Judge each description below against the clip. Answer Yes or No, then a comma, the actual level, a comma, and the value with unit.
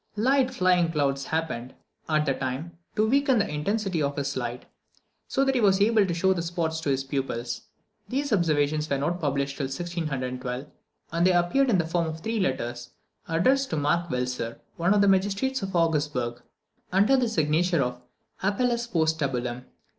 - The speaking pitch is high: No, medium, 165 Hz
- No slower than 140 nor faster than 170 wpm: No, average, 180 wpm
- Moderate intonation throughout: No, wide, 6.2 semitones